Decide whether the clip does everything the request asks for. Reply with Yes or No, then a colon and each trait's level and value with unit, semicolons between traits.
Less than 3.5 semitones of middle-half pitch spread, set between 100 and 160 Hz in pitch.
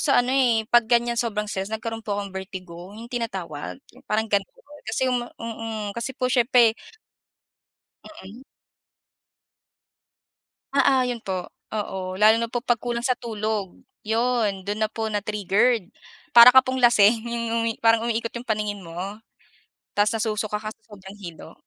No: narrow, 2.6 semitones; high, 220 Hz